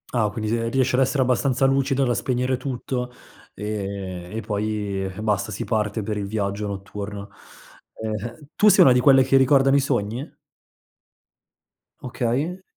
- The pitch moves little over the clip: No, average, 4.3 semitones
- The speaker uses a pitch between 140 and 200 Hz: No, low, 115 Hz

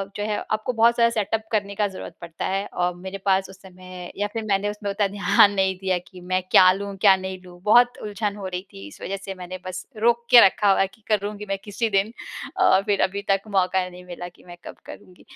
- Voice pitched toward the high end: Yes, high, 195 Hz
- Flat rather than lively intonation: Yes, narrow, 2.0 semitones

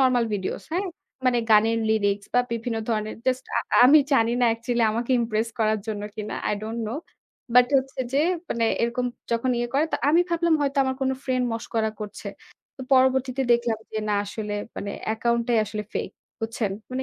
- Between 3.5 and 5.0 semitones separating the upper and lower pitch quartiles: No, average, 2.8 semitones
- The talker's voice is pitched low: No, high, 235 Hz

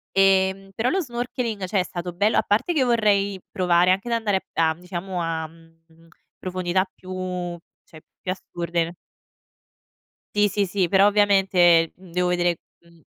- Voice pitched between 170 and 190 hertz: Yes, medium, 185 Hz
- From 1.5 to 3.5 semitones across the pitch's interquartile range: Yes, average, 2.7 semitones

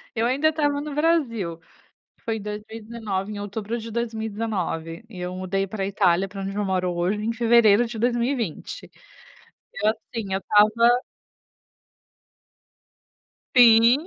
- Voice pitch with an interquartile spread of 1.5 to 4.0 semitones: Yes, average, 3.2 semitones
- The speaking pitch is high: Yes, high, 220 Hz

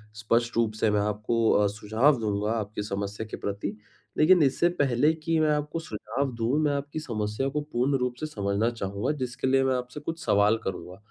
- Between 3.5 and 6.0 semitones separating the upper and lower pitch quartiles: Yes, average, 5.1 semitones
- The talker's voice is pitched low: Yes, low, 115 Hz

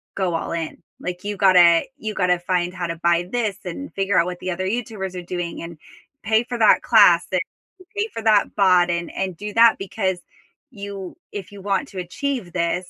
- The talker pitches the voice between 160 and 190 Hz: Yes, medium, 185 Hz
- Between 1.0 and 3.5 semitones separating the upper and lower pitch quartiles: Yes, average, 2.9 semitones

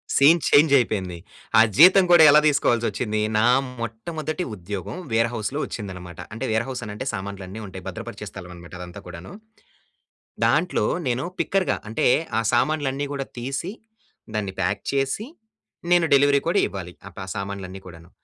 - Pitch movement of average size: No, wide, 6.7 semitones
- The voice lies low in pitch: Yes, low, 115 Hz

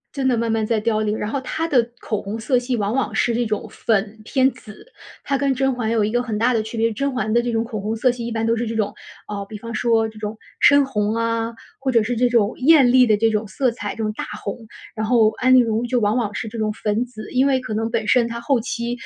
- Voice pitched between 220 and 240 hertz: Yes, high, 230 Hz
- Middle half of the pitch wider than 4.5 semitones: No, narrow, 2.4 semitones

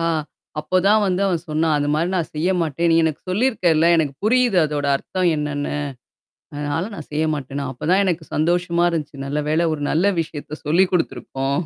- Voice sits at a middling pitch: Yes, medium, 160 Hz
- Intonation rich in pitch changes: No, average, 3.3 semitones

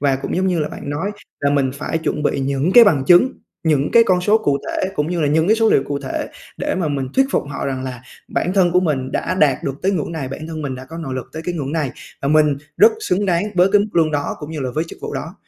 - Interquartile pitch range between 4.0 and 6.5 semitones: Yes, average, 4.5 semitones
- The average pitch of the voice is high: No, medium, 155 Hz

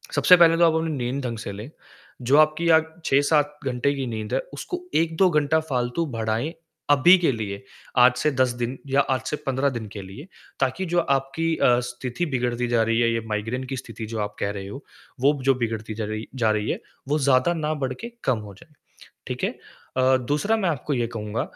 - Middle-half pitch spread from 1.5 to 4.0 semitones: No, average, 4.9 semitones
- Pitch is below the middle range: Yes, low, 130 Hz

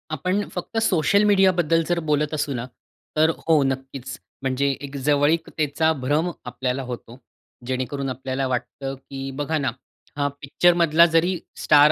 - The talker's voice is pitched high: No, medium, 145 Hz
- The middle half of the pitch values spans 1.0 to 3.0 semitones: No, average, 3.6 semitones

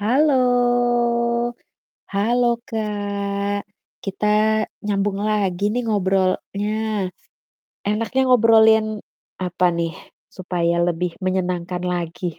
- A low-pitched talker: No, high, 205 Hz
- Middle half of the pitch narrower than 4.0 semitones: Yes, average, 2.8 semitones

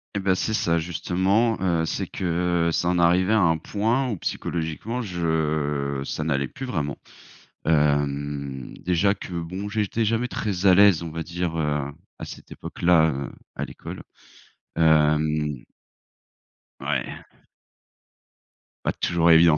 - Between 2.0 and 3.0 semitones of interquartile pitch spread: No, average, 4.0 semitones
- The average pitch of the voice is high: No, very low, 85 Hz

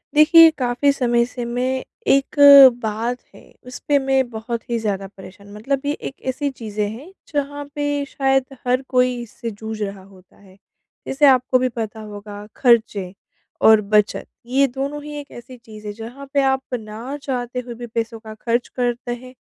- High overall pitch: Yes, high, 245 Hz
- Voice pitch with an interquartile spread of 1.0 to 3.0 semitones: No, average, 3.5 semitones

